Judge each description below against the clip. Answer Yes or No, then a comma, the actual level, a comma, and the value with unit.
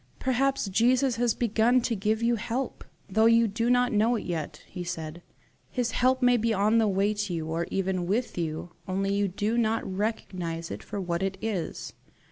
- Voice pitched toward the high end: Yes, high, 210 Hz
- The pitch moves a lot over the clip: No, average, 4.0 semitones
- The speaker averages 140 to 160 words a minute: No, average, 195 wpm